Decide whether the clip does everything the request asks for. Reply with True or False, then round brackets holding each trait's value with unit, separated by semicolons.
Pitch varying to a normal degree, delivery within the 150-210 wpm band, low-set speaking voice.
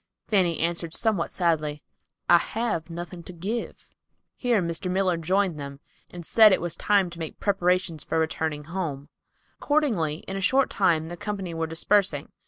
False (3.2 semitones; 160 wpm; 175 Hz)